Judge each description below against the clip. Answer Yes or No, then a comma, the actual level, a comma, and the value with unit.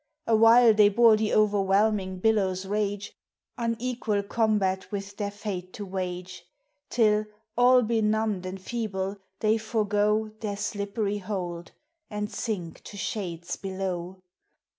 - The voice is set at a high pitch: Yes, high, 205 Hz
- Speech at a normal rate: No, slow, 120 wpm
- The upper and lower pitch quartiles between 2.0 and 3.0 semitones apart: Yes, narrow, 2.4 semitones